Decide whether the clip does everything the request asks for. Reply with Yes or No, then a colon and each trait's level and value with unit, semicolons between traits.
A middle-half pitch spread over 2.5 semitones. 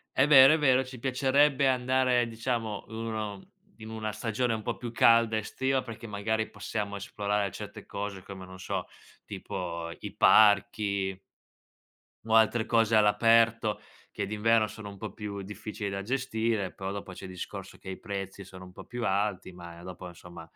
Yes: average, 2.9 semitones